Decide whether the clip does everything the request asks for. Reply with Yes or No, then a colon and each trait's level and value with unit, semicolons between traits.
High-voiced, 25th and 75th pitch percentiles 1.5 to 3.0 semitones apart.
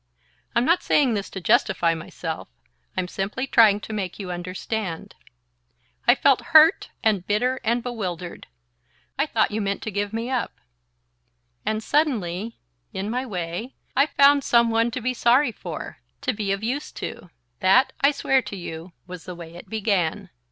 No: high, 215 Hz; average, 5.2 semitones